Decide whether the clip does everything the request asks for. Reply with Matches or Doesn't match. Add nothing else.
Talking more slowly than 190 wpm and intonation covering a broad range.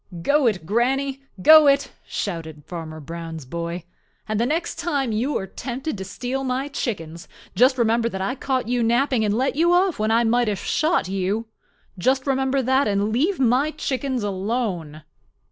Matches